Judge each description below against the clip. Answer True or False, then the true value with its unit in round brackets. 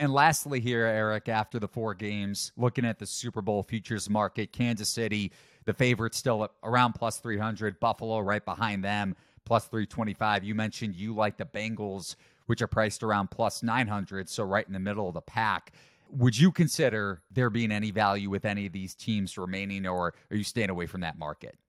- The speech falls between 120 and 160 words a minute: False (195 wpm)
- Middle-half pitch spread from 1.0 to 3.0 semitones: True (2.4 semitones)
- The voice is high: False (110 Hz)